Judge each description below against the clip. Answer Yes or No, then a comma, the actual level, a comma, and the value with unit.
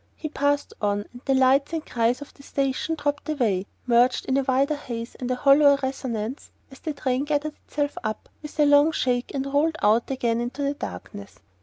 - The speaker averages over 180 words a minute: Yes, average, 200 wpm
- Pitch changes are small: No, average, 3.0 semitones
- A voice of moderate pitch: No, very high, 270 Hz